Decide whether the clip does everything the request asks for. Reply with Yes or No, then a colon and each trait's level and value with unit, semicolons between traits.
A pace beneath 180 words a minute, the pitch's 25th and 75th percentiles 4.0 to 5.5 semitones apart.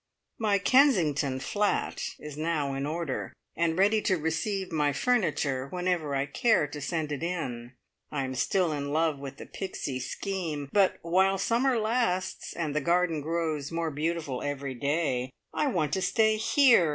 Yes: average, 165 wpm; average, 4.9 semitones